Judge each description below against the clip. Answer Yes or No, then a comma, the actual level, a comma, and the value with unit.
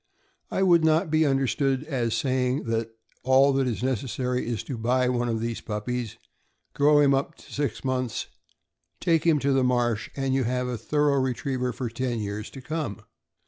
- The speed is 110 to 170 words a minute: No, average, 185 wpm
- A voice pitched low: Yes, low, 130 Hz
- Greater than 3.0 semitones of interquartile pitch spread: No, average, 2.7 semitones